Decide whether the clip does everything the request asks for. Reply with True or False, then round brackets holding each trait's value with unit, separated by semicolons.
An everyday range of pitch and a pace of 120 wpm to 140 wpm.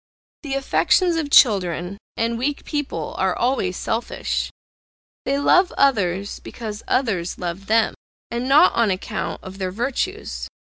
False (6.5 semitones; 135 wpm)